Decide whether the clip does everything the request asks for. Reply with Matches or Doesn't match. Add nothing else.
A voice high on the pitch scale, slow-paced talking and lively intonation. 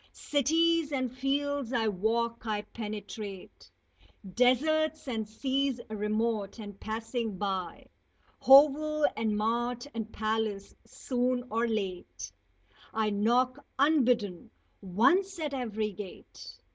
Doesn't match